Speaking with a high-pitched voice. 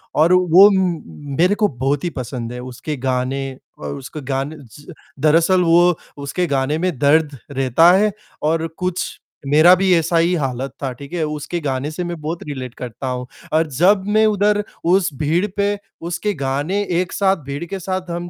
No: medium, 160 Hz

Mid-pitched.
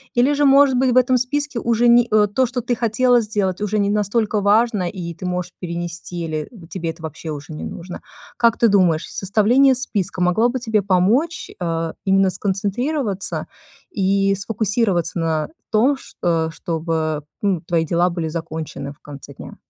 No: high, 195 Hz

